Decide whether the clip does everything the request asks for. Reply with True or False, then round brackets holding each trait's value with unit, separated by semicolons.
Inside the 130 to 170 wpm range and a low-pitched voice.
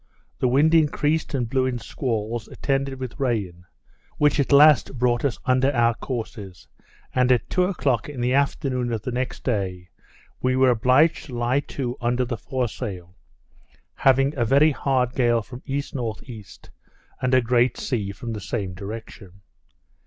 True (160 wpm; 125 Hz)